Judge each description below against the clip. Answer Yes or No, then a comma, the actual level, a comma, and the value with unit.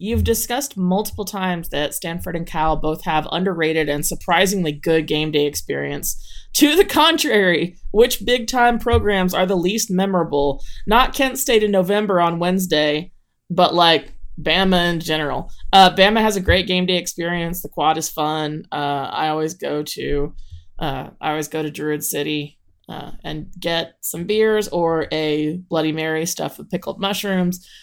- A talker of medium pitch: Yes, medium, 170 Hz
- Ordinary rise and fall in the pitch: Yes, average, 4.1 semitones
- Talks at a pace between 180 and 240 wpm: No, average, 165 wpm